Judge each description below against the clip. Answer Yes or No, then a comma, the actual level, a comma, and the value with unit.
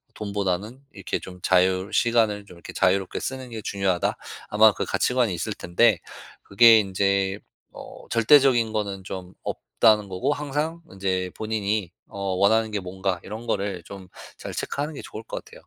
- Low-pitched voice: Yes, low, 100 Hz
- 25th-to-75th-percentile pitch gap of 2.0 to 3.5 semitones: Yes, average, 3.0 semitones